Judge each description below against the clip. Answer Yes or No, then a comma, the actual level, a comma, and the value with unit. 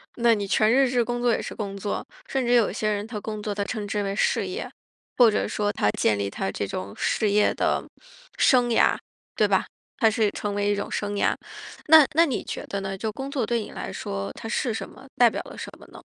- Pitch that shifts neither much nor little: Yes, average, 3.0 semitones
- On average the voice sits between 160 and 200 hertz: No, high, 215 Hz